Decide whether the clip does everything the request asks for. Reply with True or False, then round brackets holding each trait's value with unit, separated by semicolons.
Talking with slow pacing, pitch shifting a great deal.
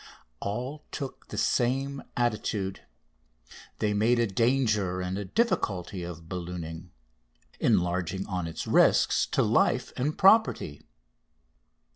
True (110 wpm; 5.7 semitones)